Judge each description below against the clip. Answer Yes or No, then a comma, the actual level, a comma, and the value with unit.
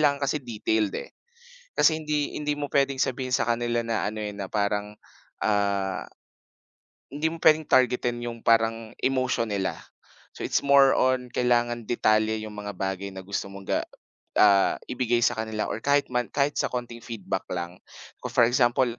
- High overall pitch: No, low, 120 Hz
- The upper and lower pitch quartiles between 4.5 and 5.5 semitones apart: No, average, 3.7 semitones